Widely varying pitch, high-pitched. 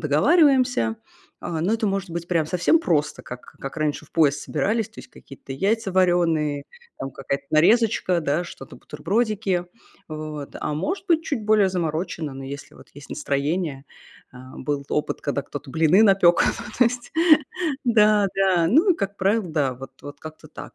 No: wide, 6.3 semitones; medium, 170 Hz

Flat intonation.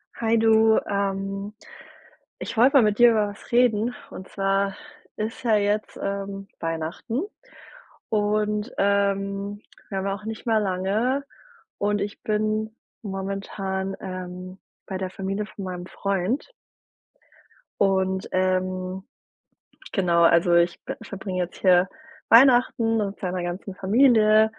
Yes: narrow, 2.3 semitones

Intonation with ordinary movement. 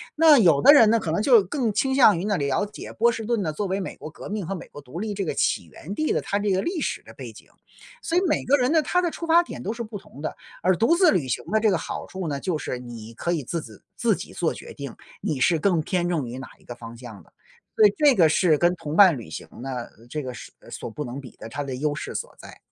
No: wide, 7.7 semitones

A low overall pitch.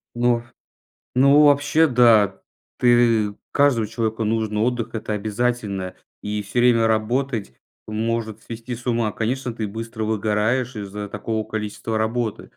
Yes: low, 115 Hz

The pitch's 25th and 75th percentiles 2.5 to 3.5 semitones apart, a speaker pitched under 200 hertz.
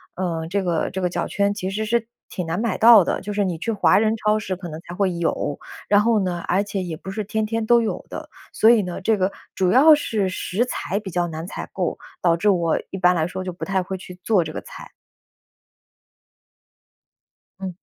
Yes: average, 3.2 semitones; high, 190 Hz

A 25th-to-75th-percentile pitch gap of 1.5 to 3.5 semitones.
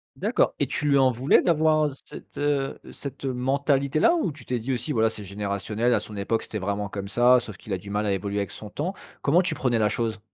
No: average, 5.2 semitones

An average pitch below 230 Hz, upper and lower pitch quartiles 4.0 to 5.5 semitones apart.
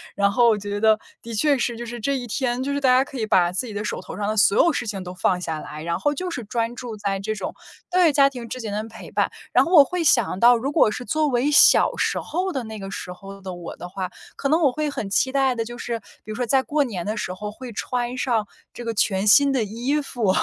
No: high, 235 Hz; average, 4.8 semitones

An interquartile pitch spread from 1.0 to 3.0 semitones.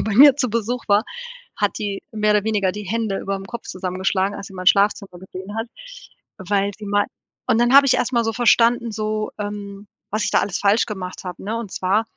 Yes: narrow, 2.4 semitones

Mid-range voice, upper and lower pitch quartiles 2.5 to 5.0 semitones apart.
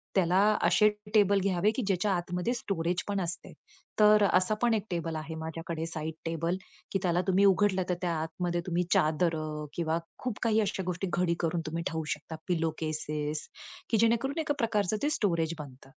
Yes: medium, 180 Hz; average, 3.8 semitones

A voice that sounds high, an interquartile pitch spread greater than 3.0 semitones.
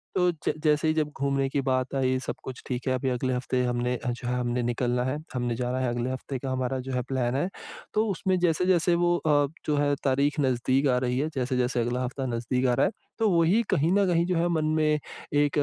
No: low, 130 Hz; average, 3.5 semitones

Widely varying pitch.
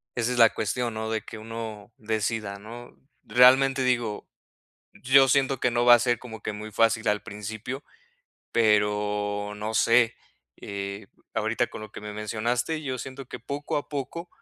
No: average, 2.9 semitones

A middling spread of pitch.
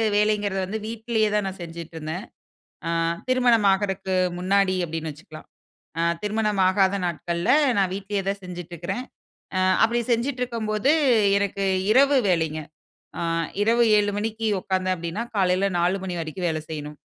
Yes: average, 3.7 semitones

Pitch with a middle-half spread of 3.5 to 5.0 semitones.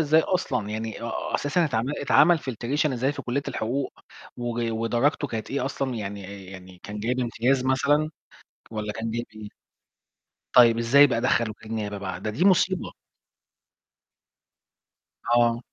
Yes: average, 4.2 semitones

